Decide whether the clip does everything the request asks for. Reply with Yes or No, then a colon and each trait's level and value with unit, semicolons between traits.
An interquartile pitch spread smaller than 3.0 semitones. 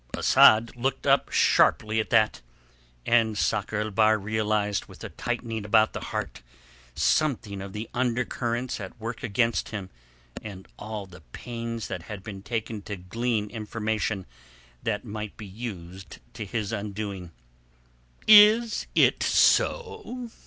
Yes: narrow, 2.4 semitones